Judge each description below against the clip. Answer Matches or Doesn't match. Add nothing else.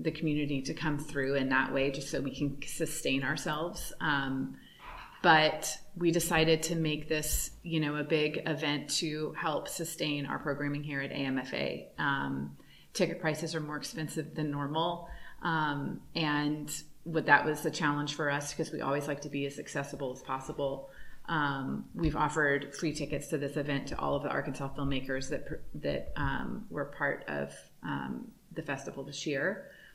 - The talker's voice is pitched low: Doesn't match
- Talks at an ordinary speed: Matches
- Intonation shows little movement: Matches